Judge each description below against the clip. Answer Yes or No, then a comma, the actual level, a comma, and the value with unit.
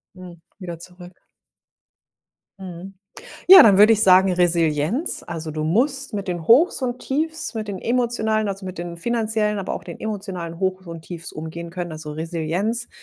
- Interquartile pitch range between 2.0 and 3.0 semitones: No, average, 4.4 semitones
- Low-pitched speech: No, medium, 185 Hz